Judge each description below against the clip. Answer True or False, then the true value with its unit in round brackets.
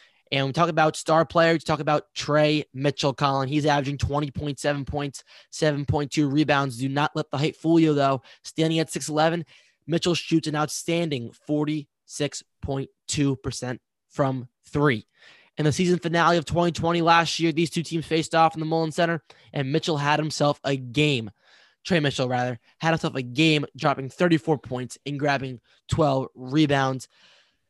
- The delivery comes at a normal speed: True (160 wpm)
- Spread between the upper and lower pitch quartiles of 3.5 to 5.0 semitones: False (2.8 semitones)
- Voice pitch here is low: False (150 Hz)